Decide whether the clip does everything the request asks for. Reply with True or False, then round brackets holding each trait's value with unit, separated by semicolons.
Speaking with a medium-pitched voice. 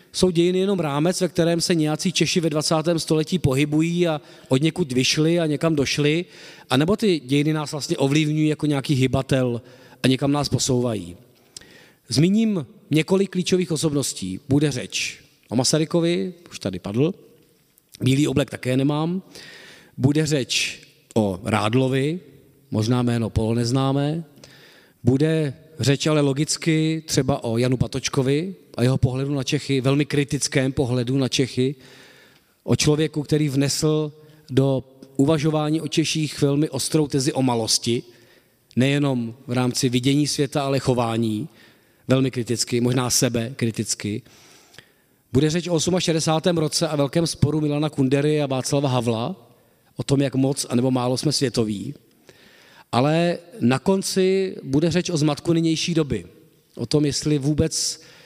True (145 Hz)